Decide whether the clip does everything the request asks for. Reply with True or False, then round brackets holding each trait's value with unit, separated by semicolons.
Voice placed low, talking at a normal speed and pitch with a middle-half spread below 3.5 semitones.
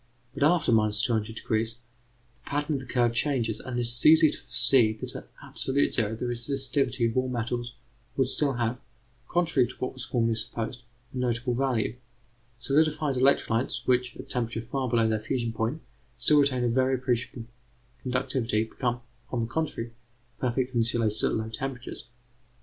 True (125 Hz; 160 wpm; 2.6 semitones)